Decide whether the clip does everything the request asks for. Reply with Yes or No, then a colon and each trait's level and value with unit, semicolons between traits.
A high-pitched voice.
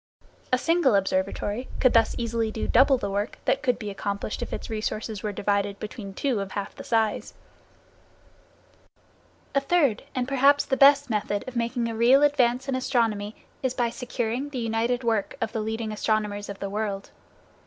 Yes: high, 230 Hz